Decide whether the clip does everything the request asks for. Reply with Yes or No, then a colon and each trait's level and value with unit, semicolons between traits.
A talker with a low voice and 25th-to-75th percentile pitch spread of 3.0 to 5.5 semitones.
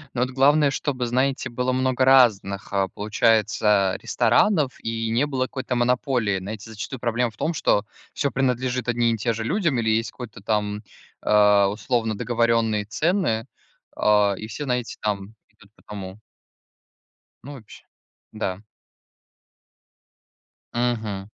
Yes: low, 115 Hz; average, 3.5 semitones